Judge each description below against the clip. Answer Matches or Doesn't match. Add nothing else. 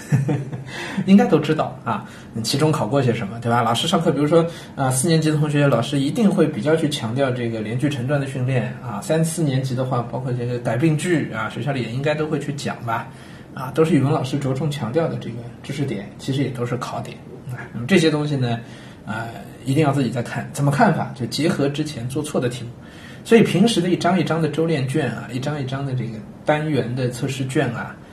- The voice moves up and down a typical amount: Matches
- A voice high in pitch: Doesn't match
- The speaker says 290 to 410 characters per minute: Matches